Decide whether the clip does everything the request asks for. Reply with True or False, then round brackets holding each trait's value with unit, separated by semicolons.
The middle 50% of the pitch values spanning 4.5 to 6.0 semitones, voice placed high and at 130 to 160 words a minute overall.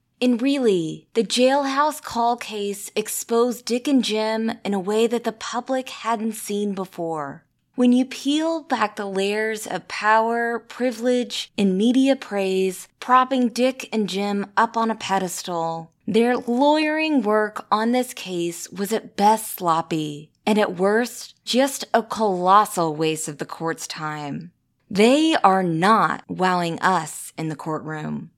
True (4.8 semitones; 215 Hz; 145 wpm)